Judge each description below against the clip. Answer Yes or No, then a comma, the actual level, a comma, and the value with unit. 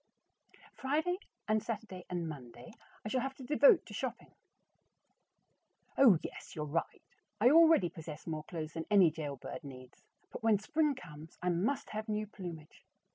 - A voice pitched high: Yes, high, 195 Hz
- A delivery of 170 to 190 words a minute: No, average, 155 wpm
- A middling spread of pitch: No, wide, 8.1 semitones